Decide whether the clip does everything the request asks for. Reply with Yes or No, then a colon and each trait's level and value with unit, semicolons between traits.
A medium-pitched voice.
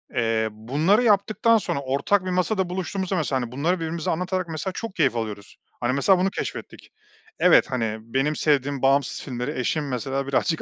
Yes: medium, 145 Hz